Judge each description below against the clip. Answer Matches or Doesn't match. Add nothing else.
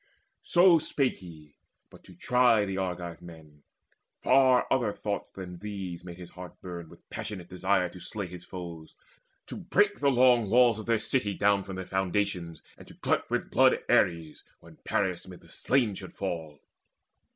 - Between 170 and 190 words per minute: Matches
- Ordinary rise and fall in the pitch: Matches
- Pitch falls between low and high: Doesn't match